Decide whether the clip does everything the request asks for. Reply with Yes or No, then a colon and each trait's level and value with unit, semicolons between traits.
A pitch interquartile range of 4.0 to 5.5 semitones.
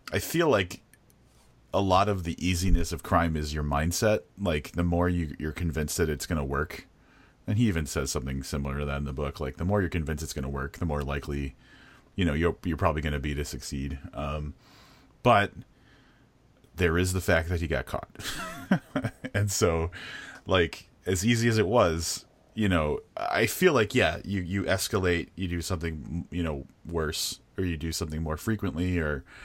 Yes: average, 4.4 semitones